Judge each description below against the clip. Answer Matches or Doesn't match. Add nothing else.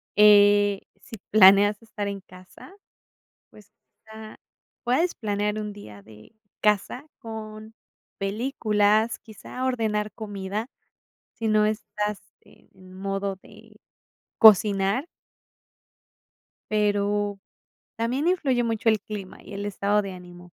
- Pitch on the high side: Matches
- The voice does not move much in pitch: Matches